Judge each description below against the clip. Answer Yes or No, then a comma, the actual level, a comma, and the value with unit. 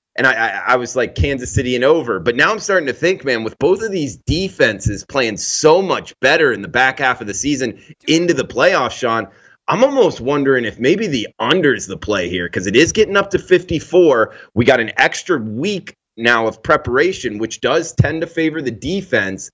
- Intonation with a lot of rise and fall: Yes, wide, 6.0 semitones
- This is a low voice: No, medium, 145 Hz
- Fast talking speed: Yes, fast, 210 wpm